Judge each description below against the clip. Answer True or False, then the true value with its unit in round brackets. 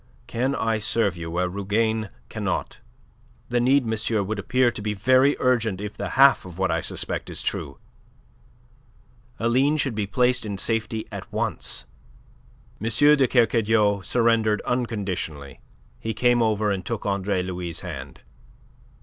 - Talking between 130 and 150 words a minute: True (145 wpm)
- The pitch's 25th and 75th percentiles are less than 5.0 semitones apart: True (3.5 semitones)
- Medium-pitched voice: False (110 Hz)